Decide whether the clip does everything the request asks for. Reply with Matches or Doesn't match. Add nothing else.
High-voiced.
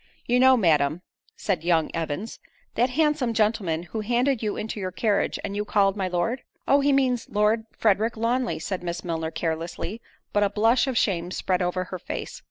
Matches